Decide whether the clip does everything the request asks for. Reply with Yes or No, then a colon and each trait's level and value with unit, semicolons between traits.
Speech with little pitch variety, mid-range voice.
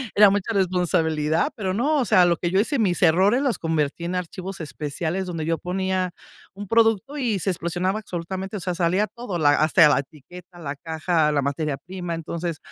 No: average, 3.1 semitones; medium, 180 Hz